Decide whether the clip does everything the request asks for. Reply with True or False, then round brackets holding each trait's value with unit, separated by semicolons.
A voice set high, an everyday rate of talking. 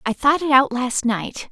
False (260 Hz; 240 wpm)